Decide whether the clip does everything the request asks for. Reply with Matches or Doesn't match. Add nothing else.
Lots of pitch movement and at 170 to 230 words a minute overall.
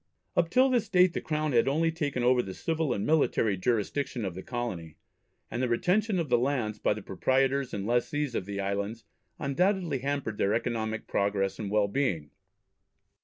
Matches